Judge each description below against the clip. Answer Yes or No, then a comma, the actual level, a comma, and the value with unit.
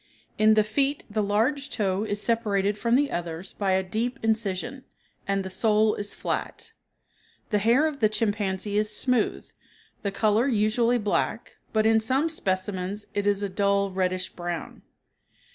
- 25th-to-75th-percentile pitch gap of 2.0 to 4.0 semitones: Yes, narrow, 2.6 semitones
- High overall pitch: Yes, high, 210 Hz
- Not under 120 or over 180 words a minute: Yes, average, 160 wpm